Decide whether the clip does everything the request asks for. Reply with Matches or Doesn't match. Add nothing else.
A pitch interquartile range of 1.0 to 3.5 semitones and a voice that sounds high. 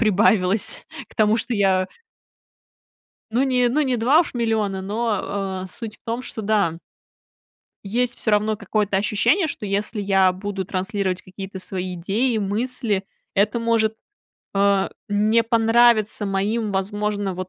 Matches